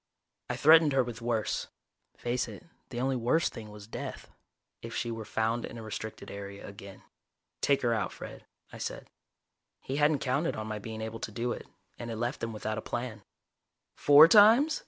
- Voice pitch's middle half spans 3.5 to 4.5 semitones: Yes, average, 3.8 semitones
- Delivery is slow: No, average, 190 wpm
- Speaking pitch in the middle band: No, low, 120 Hz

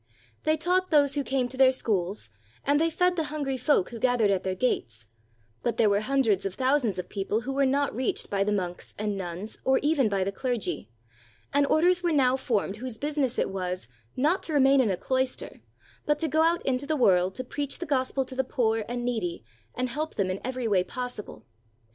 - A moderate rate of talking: No, fast, 220 wpm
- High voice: Yes, very high, 255 Hz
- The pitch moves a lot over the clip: Yes, wide, 5.8 semitones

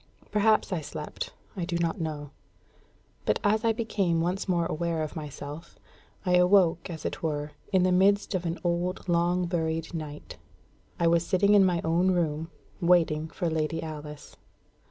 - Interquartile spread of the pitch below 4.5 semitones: Yes, narrow, 2.4 semitones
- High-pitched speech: No, medium, 170 Hz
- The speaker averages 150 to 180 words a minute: Yes, average, 165 wpm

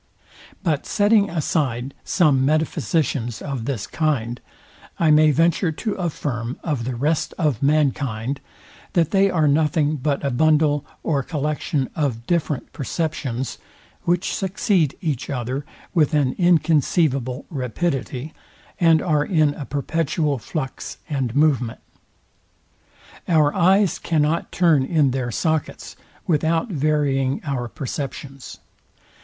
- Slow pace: Yes, slow, 115 wpm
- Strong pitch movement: No, average, 3.3 semitones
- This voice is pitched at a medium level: Yes, medium, 150 Hz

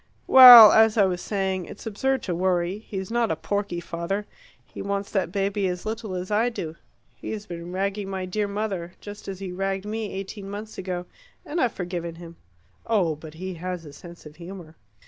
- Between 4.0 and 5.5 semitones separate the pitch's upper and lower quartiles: No, average, 2.9 semitones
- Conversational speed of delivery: Yes, average, 195 wpm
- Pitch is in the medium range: No, high, 195 Hz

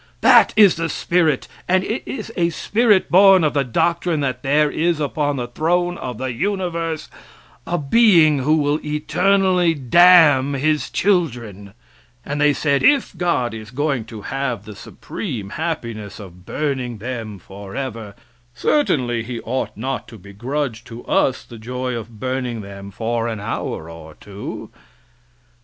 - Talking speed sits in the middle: Yes, average, 150 wpm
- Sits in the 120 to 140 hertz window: Yes, low, 135 Hz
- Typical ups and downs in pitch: No, wide, 6.4 semitones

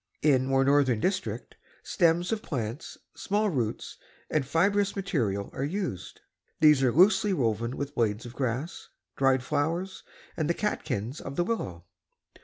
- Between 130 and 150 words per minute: Yes, average, 145 wpm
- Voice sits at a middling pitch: Yes, medium, 145 Hz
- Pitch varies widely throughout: Yes, wide, 6.8 semitones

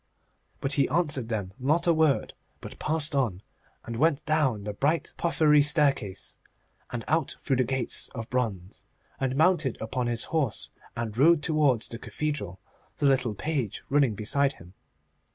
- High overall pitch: No, low, 135 Hz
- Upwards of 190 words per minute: No, average, 155 wpm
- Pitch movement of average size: Yes, average, 4.9 semitones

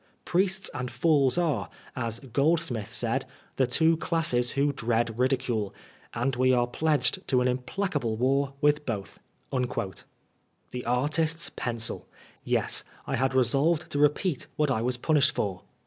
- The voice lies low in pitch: Yes, low, 130 Hz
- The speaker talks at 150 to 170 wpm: No, average, 140 wpm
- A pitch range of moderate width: Yes, average, 3.8 semitones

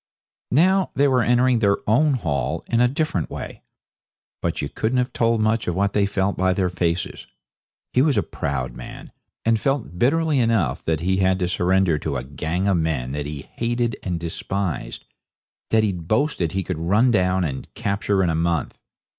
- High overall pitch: No, very low, 95 Hz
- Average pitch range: No, wide, 5.8 semitones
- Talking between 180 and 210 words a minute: Yes, average, 190 wpm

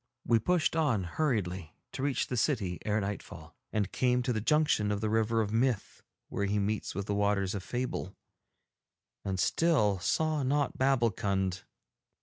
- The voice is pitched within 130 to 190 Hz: No, low, 110 Hz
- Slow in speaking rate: No, average, 160 wpm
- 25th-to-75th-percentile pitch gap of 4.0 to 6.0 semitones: Yes, average, 4.7 semitones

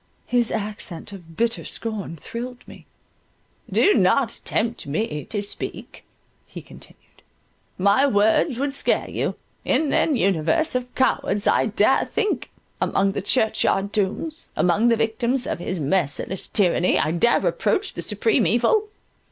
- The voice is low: No, high, 220 Hz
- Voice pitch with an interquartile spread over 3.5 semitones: Yes, average, 4.7 semitones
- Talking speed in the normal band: No, slow, 130 wpm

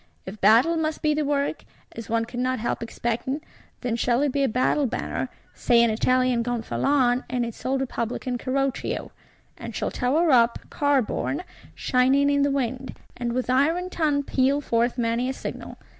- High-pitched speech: Yes, very high, 255 Hz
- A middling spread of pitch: Yes, average, 3.0 semitones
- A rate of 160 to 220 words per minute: Yes, average, 175 wpm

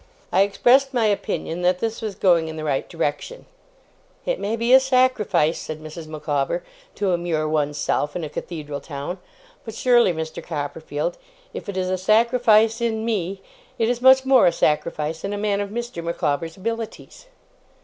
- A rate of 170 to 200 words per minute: Yes, average, 175 wpm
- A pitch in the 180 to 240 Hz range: Yes, medium, 185 Hz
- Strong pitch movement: Yes, wide, 6.3 semitones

